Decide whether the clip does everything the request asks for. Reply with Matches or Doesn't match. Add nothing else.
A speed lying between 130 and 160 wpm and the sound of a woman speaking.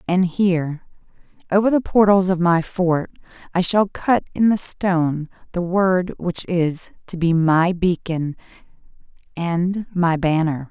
Matches